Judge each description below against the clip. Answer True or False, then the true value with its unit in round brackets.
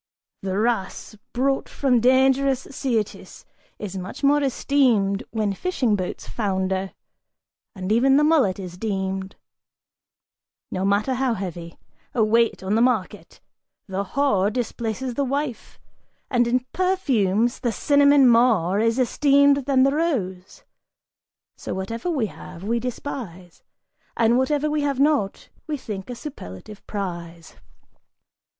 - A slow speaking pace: True (130 wpm)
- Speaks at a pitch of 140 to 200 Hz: False (230 Hz)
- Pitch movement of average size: False (5.7 semitones)